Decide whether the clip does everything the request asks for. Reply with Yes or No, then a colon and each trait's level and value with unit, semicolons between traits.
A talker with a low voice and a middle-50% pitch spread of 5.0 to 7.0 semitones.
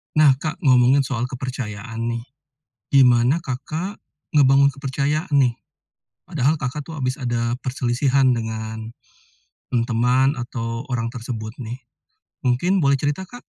No: low, 130 Hz; average, 2.9 semitones